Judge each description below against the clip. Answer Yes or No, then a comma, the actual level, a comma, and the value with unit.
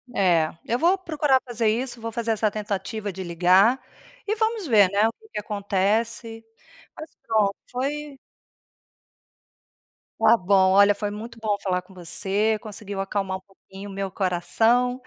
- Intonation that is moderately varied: Yes, average, 3.5 semitones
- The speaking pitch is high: Yes, high, 210 Hz